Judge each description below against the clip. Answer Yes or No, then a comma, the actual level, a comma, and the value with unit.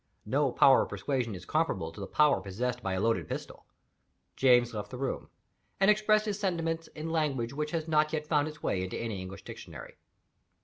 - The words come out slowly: No, average, 195 wpm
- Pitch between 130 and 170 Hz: Yes, medium, 140 Hz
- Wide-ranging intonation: Yes, wide, 6.8 semitones